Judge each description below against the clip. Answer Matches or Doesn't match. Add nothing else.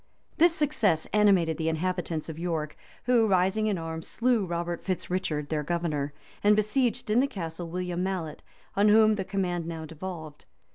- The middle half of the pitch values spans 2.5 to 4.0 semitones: Doesn't match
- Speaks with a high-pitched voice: Doesn't match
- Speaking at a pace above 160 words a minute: Matches